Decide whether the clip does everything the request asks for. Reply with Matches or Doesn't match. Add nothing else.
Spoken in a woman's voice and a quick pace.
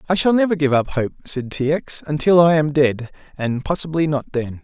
Doesn't match